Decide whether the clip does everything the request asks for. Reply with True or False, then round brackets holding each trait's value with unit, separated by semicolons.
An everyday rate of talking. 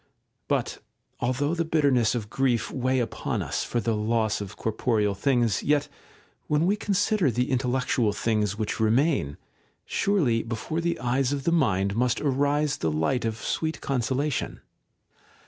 True (155 wpm)